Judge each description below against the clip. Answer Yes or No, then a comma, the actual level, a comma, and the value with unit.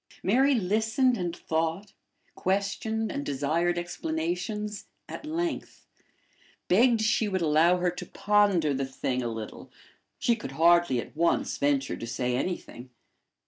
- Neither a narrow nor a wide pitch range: No, wide, 5.7 semitones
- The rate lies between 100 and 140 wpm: Yes, slow, 135 wpm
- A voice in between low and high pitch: Yes, medium, 175 Hz